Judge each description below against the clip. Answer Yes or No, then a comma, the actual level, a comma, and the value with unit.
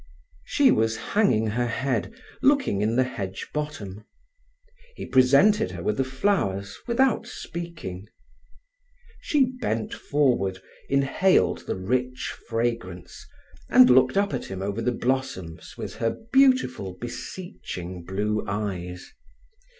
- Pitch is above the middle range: No, low, 120 Hz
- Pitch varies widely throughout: Yes, wide, 7.2 semitones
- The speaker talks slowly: Yes, slow, 120 wpm